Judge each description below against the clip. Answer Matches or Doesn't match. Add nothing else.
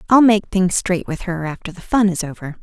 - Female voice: Matches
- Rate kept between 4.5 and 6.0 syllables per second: Matches